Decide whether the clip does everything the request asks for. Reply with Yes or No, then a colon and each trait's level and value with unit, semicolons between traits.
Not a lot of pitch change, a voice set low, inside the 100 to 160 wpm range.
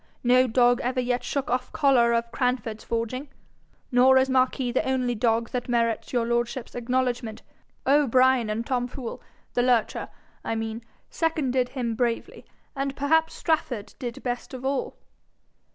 No: narrow, 1.9 semitones; very high, 250 Hz; average, 150 wpm